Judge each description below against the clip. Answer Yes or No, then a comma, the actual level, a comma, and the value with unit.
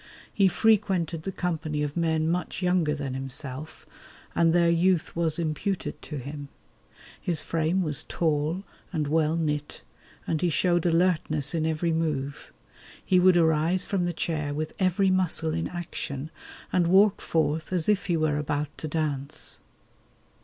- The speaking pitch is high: No, medium, 160 Hz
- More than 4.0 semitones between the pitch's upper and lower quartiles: No, average, 2.7 semitones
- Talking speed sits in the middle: Yes, average, 155 wpm